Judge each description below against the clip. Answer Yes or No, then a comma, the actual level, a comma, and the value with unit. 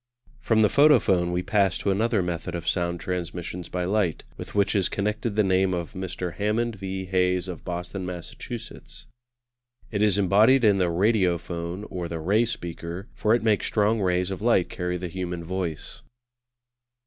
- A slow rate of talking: No, average, 170 wpm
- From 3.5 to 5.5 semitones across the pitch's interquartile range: No, average, 2.9 semitones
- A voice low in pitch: Yes, very low, 95 Hz